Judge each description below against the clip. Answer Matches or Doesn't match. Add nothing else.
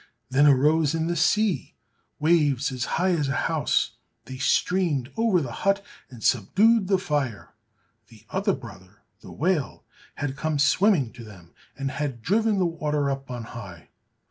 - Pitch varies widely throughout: Matches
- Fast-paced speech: Doesn't match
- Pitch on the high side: Doesn't match